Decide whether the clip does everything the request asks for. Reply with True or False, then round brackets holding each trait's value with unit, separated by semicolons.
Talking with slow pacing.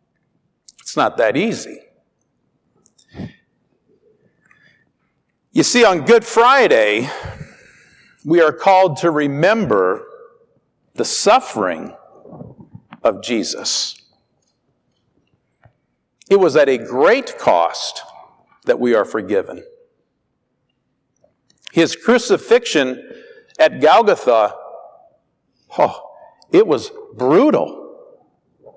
True (75 wpm)